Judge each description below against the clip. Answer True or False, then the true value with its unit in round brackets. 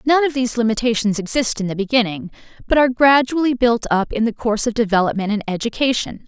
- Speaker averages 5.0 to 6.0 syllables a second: False (6.5 syllables/s)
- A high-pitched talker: True (235 Hz)